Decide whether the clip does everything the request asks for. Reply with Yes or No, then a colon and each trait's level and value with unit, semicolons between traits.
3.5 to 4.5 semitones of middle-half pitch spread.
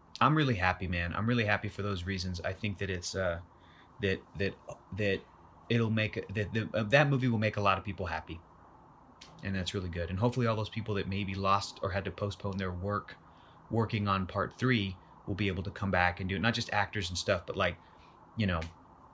No: average, 3.0 semitones